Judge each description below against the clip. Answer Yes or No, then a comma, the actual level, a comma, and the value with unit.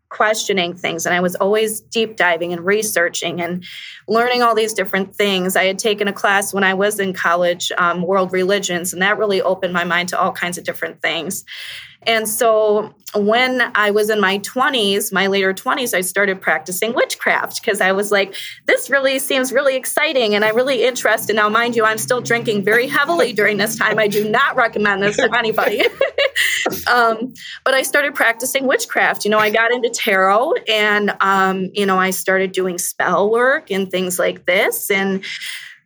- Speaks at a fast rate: No, average, 190 wpm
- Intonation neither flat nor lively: Yes, average, 3.8 semitones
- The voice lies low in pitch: No, high, 210 Hz